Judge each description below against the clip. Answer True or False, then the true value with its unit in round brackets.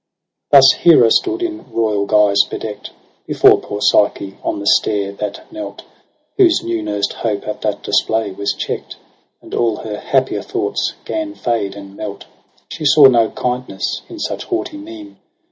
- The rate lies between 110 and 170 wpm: True (160 wpm)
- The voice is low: True (115 Hz)